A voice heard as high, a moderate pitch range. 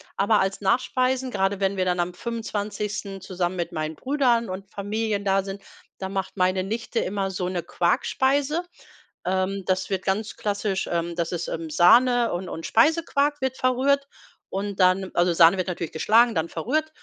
Yes: high, 195 Hz; average, 4.3 semitones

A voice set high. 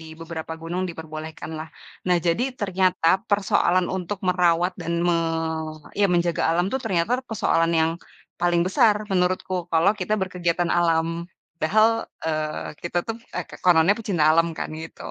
No: medium, 175 Hz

